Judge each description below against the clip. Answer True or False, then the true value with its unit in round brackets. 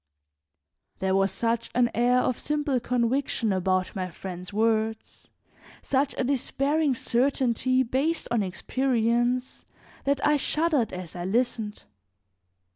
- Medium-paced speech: False (120 wpm)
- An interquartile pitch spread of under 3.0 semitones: False (3.9 semitones)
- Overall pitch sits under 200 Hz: False (240 Hz)